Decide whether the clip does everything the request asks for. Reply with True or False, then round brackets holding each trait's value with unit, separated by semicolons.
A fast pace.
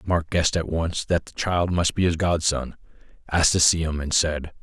True (220 wpm)